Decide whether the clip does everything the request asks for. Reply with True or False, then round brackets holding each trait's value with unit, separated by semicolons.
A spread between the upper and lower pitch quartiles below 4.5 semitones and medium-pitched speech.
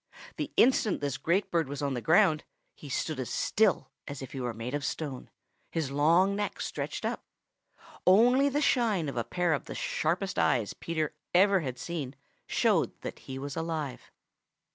False (5.6 semitones; 155 Hz)